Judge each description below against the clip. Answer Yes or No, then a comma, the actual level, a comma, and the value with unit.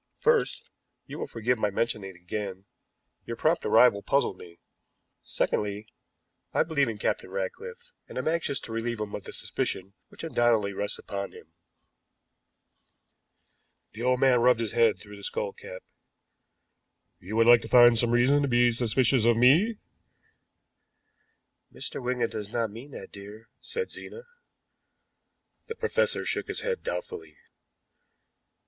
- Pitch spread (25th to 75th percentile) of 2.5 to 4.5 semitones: No, average, 5.2 semitones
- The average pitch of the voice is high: No, low, 120 Hz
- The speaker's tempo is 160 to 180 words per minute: No, average, 145 wpm